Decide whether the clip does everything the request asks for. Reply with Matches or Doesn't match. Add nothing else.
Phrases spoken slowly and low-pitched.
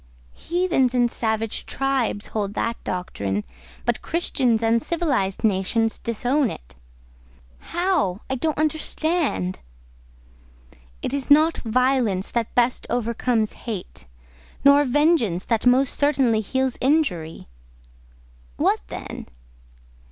Doesn't match